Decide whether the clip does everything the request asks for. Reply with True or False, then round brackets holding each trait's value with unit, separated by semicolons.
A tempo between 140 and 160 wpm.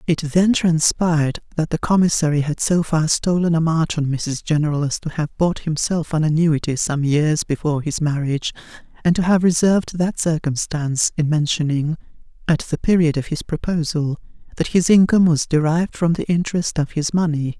False (175 wpm)